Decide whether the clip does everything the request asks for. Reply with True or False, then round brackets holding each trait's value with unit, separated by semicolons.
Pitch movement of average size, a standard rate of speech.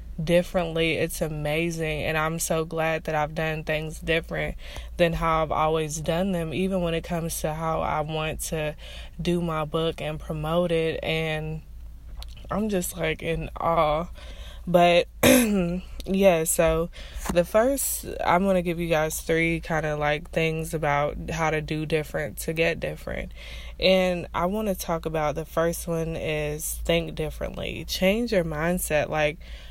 False (1.9 semitones; 160 wpm)